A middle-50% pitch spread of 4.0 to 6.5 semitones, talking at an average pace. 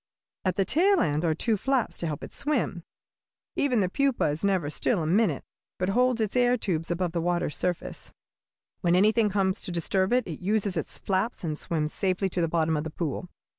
No: average, 4.8 semitones; fast, 210 wpm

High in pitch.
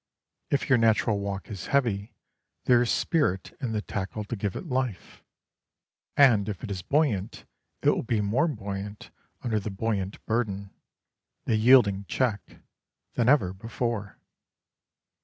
No: low, 110 Hz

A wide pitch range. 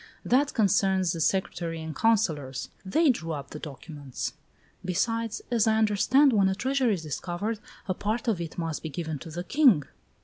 Yes: wide, 5.7 semitones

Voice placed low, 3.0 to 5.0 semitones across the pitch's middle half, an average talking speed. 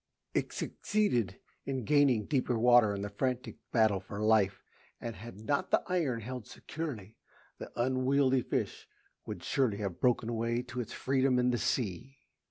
Yes: low, 120 Hz; average, 3.5 semitones; average, 160 wpm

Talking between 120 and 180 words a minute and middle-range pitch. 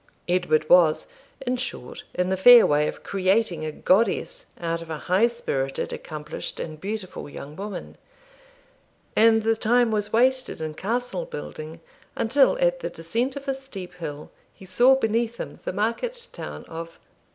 No: average, 160 wpm; high, 205 Hz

